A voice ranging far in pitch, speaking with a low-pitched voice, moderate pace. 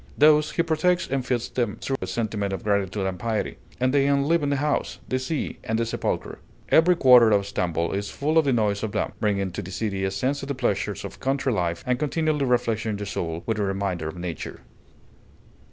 No: wide, 5.9 semitones; low, 115 Hz; fast, 215 wpm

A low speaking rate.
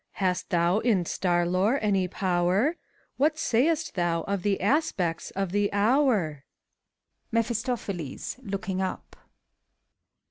Yes: slow, 115 wpm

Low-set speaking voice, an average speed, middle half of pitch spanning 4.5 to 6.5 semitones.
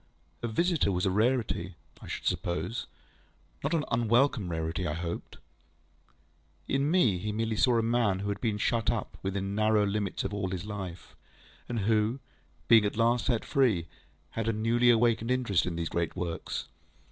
No: low, 110 Hz; average, 170 wpm; average, 3.8 semitones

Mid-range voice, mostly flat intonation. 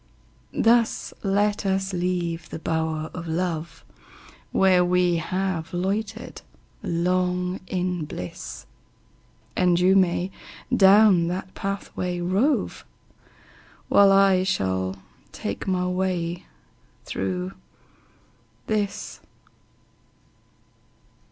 Yes: medium, 180 Hz; narrow, 2.3 semitones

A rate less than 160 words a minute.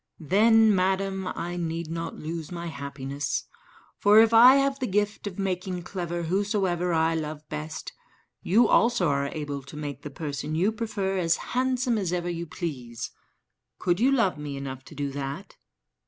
No: average, 170 wpm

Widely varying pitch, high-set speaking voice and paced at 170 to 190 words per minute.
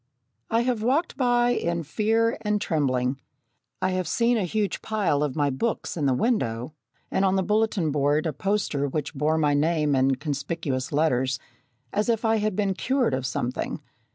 No: wide, 7.2 semitones; medium, 170 Hz; average, 180 wpm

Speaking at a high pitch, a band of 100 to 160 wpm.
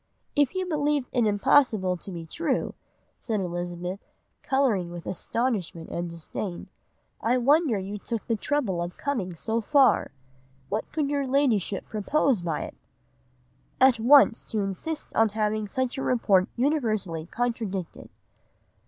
Yes: high, 220 Hz; slow, 135 wpm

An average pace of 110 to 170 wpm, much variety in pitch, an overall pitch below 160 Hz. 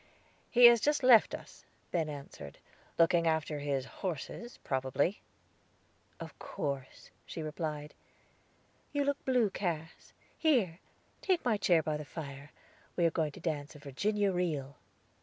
No: average, 140 wpm; wide, 6.2 semitones; medium, 165 Hz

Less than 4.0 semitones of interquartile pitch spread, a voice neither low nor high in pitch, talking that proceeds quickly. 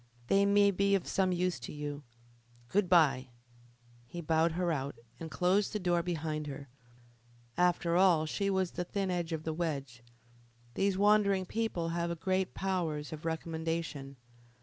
No: average, 3.2 semitones; medium, 170 Hz; average, 155 wpm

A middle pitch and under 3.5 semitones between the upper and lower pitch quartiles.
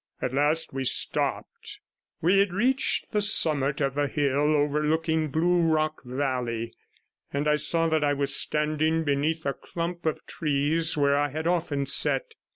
Yes: medium, 150 Hz; narrow, 2.5 semitones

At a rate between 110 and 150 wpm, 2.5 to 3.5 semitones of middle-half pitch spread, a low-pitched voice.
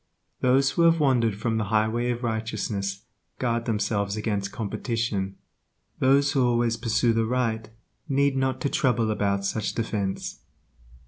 Yes: average, 140 wpm; average, 3.0 semitones; low, 115 Hz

